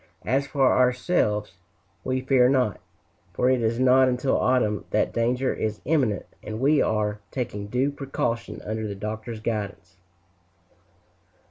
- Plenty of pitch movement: No, average, 3.4 semitones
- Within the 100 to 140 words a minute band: Yes, slow, 135 wpm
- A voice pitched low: Yes, low, 125 Hz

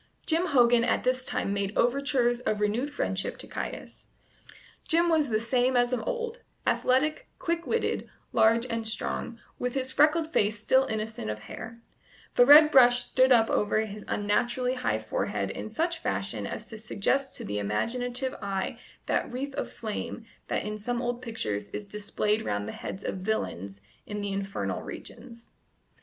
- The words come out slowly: No, average, 170 wpm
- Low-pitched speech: No, high, 240 Hz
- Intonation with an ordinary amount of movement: Yes, average, 4.0 semitones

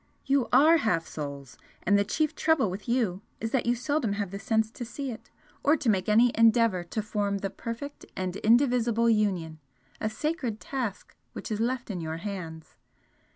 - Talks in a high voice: Yes, high, 220 Hz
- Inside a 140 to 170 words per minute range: No, average, 185 wpm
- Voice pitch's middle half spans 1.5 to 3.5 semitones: No, average, 4.0 semitones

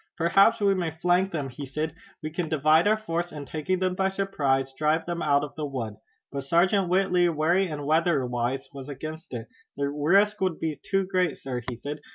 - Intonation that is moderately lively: Yes, average, 4.4 semitones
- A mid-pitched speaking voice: Yes, medium, 160 Hz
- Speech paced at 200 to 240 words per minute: Yes, fast, 205 wpm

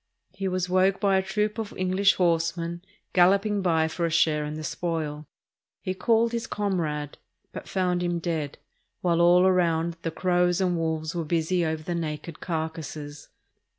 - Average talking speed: Yes, average, 170 wpm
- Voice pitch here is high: No, medium, 175 Hz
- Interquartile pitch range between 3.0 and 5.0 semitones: No, narrow, 2.6 semitones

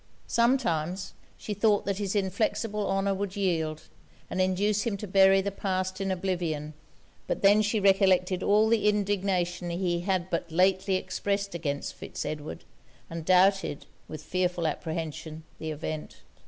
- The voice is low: No, medium, 185 Hz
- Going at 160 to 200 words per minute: No, average, 145 wpm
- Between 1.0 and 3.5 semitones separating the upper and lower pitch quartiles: Yes, narrow, 2.6 semitones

